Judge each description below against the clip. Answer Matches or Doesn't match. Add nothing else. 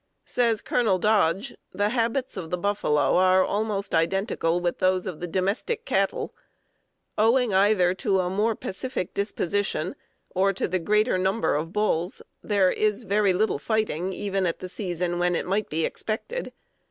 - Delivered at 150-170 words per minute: Matches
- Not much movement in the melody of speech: Doesn't match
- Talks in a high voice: Matches